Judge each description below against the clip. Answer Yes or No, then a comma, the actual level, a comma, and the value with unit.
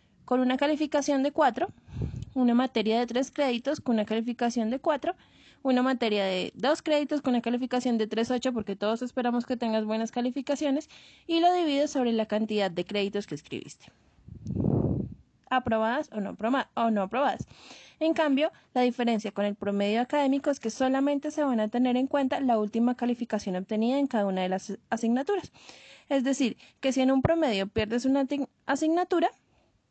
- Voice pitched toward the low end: No, very high, 250 Hz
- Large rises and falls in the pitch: No, average, 4.1 semitones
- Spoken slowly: No, average, 165 wpm